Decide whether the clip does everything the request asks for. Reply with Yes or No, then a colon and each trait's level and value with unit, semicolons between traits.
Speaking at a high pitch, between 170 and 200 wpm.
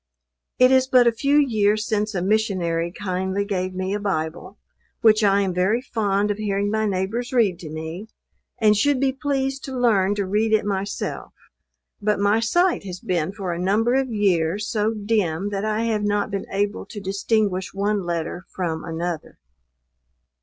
Yes: high, 205 Hz; average, 175 wpm